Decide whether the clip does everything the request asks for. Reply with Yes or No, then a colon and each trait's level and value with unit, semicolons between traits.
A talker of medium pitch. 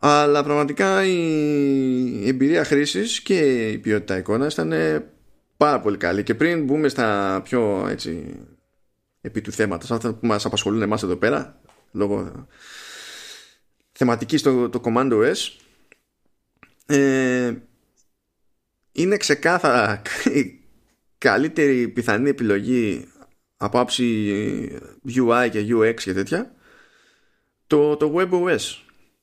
No: low, 125 Hz